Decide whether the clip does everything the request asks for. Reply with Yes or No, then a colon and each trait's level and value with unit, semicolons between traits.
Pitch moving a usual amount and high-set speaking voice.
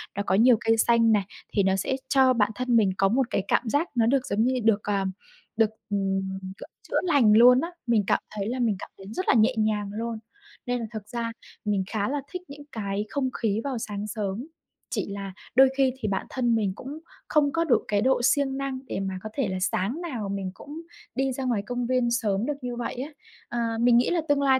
Yes: average, 4.2 semitones; high, 235 Hz